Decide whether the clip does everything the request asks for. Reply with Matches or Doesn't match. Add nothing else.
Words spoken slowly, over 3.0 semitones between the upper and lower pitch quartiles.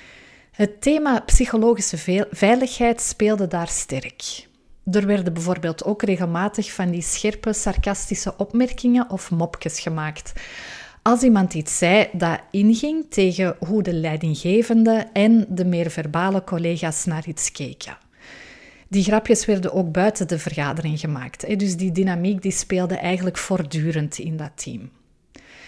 Matches